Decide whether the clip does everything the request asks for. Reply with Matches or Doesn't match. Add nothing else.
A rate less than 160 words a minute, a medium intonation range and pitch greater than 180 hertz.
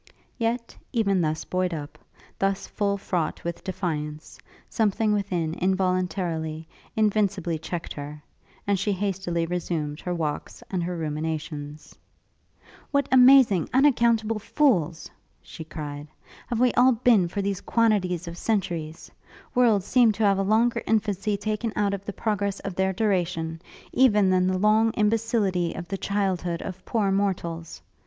Matches